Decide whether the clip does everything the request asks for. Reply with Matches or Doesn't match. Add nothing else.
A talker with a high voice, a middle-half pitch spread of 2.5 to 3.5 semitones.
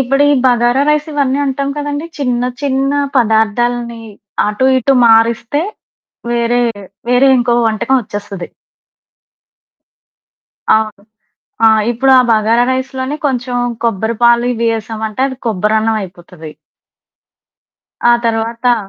Matches